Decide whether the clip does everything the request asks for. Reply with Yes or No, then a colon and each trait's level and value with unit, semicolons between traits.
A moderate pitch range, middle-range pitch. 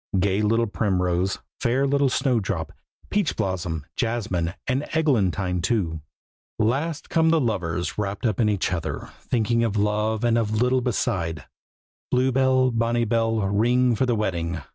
No: average, 4.7 semitones; low, 110 Hz